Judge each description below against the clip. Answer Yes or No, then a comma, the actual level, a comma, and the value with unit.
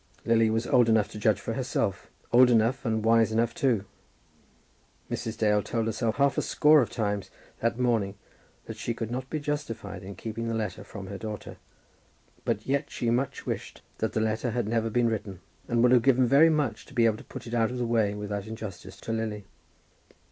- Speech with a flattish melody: Yes, narrow, 2.2 semitones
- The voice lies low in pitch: Yes, low, 115 Hz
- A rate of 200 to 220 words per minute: Yes, fast, 205 wpm